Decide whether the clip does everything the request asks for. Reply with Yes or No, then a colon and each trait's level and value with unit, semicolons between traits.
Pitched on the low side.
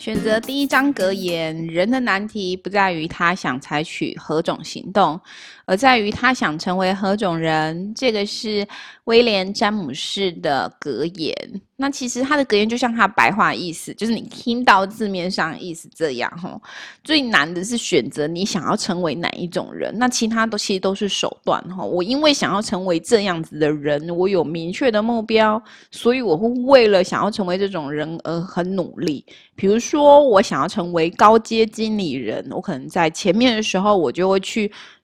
No: high, 200 Hz